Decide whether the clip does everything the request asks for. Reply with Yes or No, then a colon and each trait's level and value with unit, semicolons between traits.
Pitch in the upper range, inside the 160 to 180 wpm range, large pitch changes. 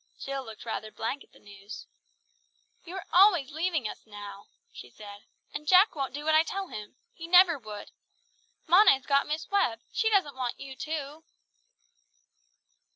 Yes: very high, 280 Hz; average, 165 wpm; wide, 7.2 semitones